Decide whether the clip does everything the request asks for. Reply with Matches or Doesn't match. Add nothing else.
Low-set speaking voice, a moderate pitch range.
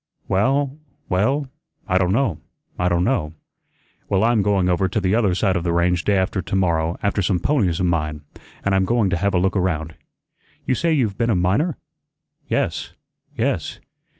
Matches